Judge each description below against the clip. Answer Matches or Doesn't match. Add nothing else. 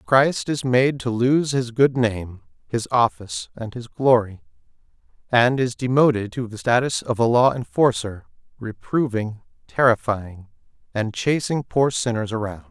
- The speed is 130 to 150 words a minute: Matches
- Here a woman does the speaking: Doesn't match